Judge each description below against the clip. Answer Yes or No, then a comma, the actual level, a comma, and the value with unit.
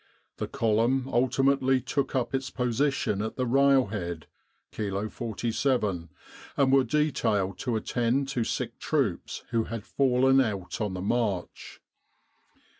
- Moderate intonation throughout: Yes, average, 4.1 semitones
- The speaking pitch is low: Yes, low, 120 Hz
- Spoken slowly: Yes, slow, 125 wpm